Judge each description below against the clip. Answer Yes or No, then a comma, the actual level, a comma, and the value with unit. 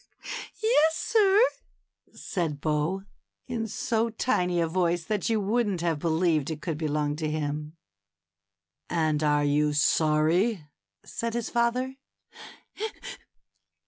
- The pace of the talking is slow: Yes, slow, 115 wpm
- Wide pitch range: Yes, wide, 7.0 semitones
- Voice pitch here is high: No, medium, 170 Hz